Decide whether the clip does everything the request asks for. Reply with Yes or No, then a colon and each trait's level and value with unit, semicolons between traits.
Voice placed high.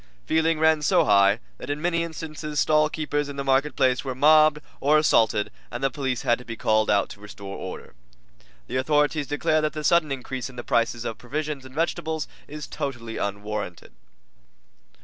No: medium, 140 Hz